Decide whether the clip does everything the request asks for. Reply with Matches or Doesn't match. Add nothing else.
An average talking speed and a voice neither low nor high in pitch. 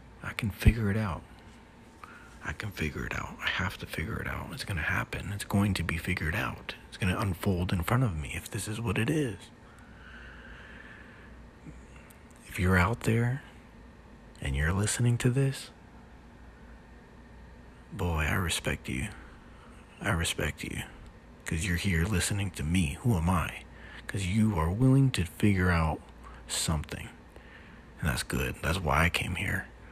Doesn't match